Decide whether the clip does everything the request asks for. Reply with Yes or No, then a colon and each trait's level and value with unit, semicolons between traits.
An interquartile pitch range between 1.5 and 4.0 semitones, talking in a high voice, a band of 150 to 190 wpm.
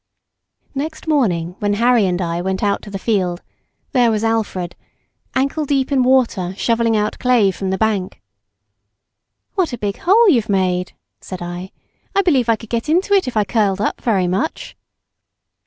No: average, 5.3 semitones; high, 220 Hz; average, 170 wpm